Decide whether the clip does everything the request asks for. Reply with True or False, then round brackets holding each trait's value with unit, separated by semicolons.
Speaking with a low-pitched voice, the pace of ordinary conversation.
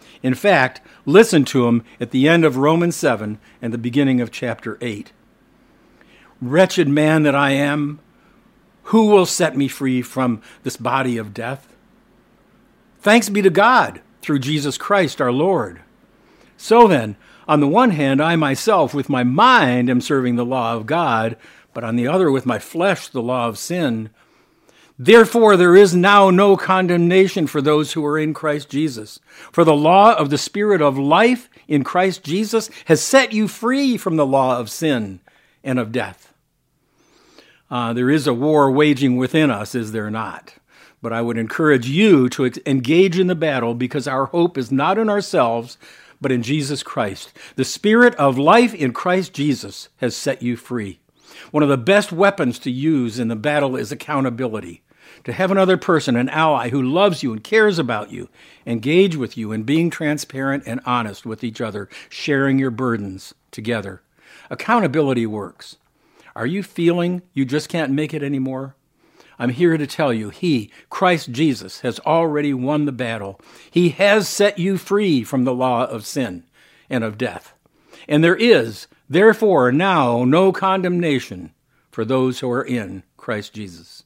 False (145 Hz; 170 wpm)